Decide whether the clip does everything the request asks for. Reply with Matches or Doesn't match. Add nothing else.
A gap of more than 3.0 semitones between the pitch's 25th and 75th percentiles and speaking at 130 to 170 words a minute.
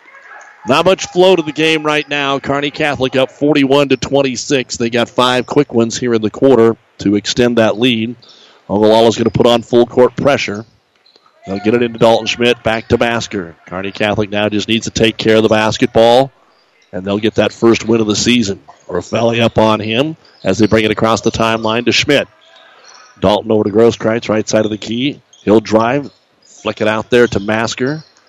Doesn't match